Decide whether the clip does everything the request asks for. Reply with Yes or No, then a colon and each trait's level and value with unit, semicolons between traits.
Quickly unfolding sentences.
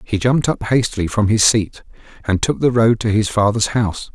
Yes: fast, 215 wpm